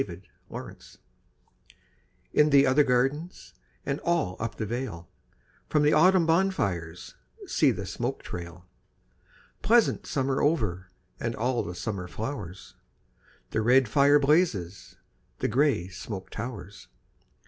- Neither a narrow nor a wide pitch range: No, wide, 7.6 semitones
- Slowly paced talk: Yes, slow, 125 wpm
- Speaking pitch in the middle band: No, low, 125 Hz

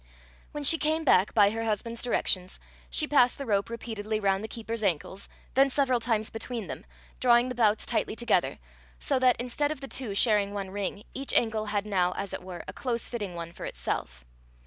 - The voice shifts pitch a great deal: No, average, 3.9 semitones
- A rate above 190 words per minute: Yes, average, 200 wpm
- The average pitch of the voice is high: Yes, high, 220 Hz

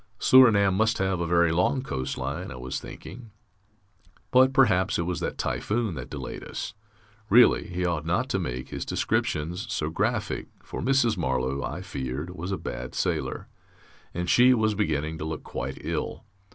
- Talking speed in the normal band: Yes, average, 170 wpm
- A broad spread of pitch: Yes, wide, 6.3 semitones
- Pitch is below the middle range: Yes, very low, 90 Hz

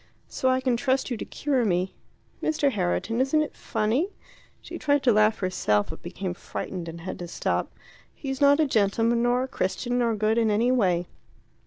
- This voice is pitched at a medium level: No, high, 230 Hz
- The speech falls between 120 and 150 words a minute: No, average, 190 wpm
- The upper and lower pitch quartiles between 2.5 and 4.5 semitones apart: No, wide, 5.5 semitones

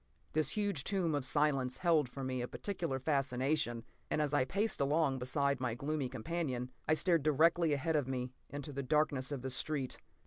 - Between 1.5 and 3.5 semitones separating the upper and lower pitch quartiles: Yes, average, 3.2 semitones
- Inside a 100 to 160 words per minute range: No, average, 185 wpm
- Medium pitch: Yes, medium, 145 Hz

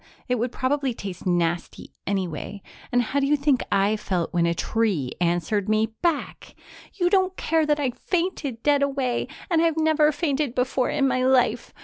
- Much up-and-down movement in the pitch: Yes, wide, 6.7 semitones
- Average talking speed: Yes, average, 175 wpm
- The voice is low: No, very high, 255 Hz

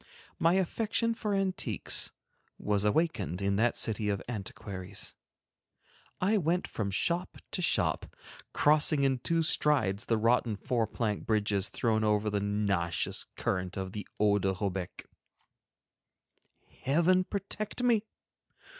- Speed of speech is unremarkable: No, slow, 125 wpm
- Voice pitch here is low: Yes, low, 110 Hz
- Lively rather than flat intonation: Yes, wide, 8.8 semitones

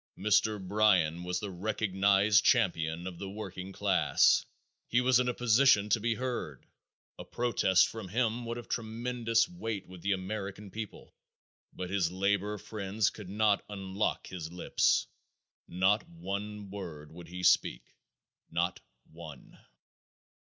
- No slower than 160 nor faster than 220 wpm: No, slow, 135 wpm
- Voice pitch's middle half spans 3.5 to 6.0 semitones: No, average, 3.1 semitones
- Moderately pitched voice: No, low, 100 Hz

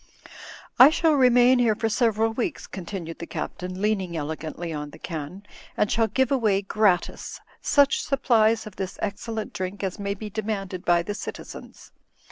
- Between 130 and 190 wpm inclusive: Yes, average, 160 wpm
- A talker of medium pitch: No, high, 205 Hz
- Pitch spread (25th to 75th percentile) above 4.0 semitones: No, average, 3.7 semitones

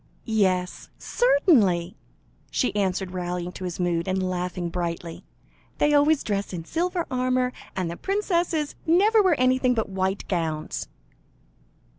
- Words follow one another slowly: Yes, slow, 130 wpm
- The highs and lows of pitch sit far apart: Yes, wide, 8.2 semitones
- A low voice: No, high, 195 Hz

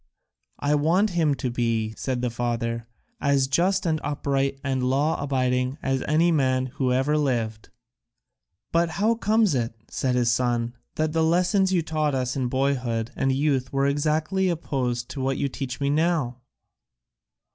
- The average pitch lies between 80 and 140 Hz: Yes, low, 135 Hz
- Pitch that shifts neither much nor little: Yes, average, 3.7 semitones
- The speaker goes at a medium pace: Yes, average, 160 wpm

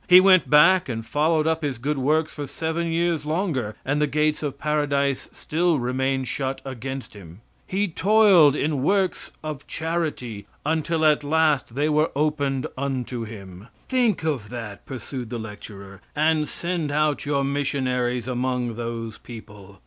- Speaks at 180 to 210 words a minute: No, average, 155 wpm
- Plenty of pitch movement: No, average, 4.3 semitones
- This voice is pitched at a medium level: Yes, medium, 145 Hz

